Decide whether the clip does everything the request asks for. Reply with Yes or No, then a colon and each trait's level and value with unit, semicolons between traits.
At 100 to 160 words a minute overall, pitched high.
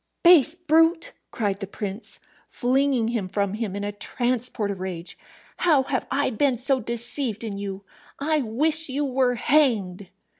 Yes: average, 155 wpm; high, 245 Hz